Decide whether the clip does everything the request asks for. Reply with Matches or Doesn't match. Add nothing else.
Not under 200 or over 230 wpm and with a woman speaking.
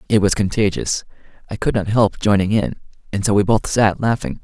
Doesn't match